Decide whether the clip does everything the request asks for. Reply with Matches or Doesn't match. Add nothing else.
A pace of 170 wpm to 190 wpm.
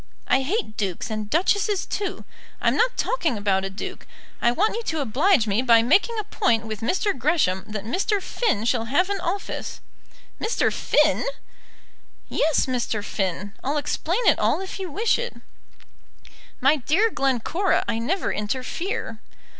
Doesn't match